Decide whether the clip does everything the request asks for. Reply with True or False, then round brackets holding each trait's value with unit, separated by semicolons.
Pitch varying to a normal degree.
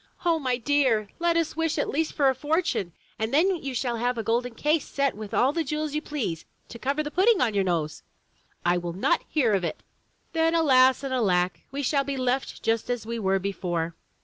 False (5.8 semitones)